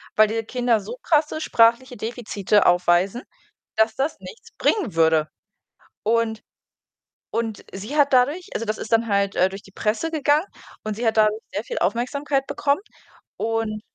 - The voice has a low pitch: No, high, 225 Hz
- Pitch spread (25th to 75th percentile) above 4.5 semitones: No, average, 3.7 semitones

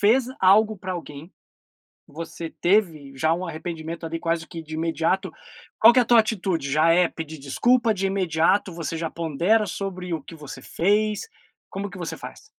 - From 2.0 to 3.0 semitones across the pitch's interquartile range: No, average, 3.7 semitones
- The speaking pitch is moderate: Yes, medium, 170 Hz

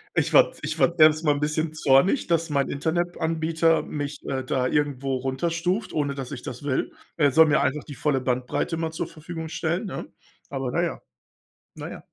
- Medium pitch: Yes, medium, 150 Hz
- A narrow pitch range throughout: No, average, 3.0 semitones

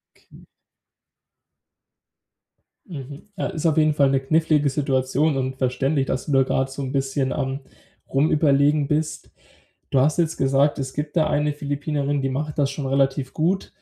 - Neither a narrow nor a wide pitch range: No, narrow, 2.1 semitones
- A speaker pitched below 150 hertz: Yes, medium, 140 Hz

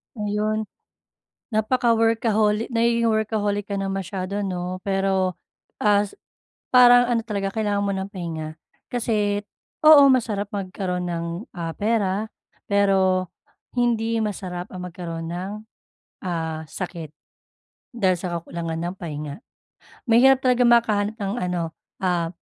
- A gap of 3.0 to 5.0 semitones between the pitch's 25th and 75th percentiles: Yes, average, 3.4 semitones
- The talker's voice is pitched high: Yes, high, 200 Hz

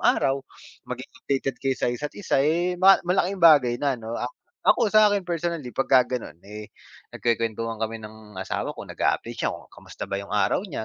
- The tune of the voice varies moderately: No, wide, 7.5 semitones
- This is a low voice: Yes, low, 130 Hz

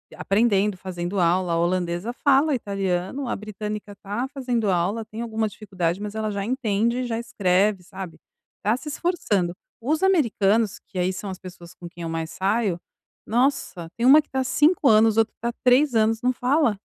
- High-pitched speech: Yes, high, 215 Hz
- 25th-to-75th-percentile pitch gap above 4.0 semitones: Yes, average, 4.6 semitones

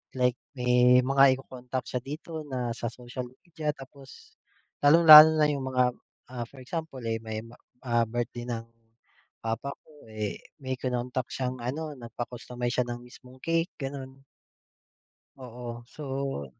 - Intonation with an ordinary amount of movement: No, narrow, 2.3 semitones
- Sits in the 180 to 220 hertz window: No, low, 125 Hz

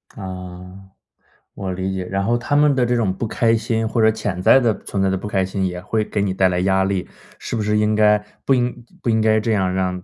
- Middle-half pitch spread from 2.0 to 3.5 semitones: Yes, average, 3.1 semitones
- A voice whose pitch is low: Yes, low, 105 Hz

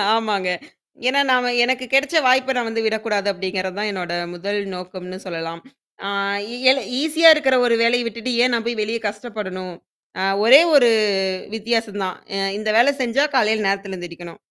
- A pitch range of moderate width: Yes, average, 4.5 semitones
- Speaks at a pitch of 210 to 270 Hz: Yes, high, 220 Hz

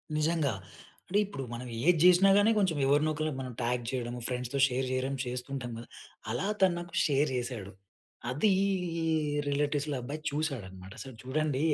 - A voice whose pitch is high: No, medium, 140 Hz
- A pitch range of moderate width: Yes, average, 3.9 semitones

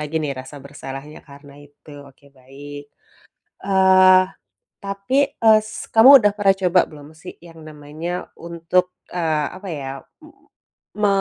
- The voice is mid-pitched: Yes, medium, 165 Hz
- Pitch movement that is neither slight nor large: Yes, average, 4.7 semitones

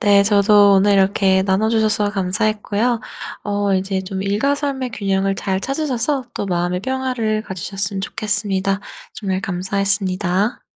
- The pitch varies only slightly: Yes, narrow, 2.3 semitones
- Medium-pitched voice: No, high, 200 Hz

